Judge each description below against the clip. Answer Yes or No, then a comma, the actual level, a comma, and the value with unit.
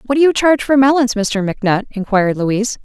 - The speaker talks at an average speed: No, fast, 210 wpm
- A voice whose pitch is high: Yes, high, 230 Hz